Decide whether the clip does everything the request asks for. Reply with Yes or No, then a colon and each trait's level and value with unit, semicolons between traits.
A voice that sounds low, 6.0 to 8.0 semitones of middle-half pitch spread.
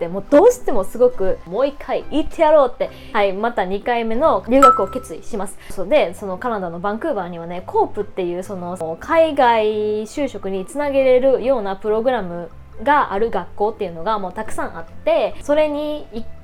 No: high, 225 Hz; wide, 6.7 semitones